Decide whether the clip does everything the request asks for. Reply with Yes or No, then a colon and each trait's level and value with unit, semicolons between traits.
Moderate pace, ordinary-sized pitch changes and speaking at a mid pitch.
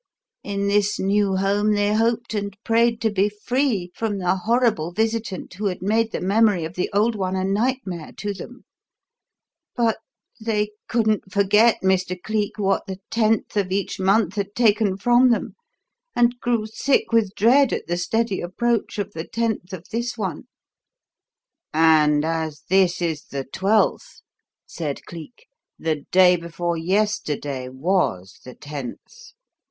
No: average, 150 wpm; average, 3.9 semitones; high, 200 Hz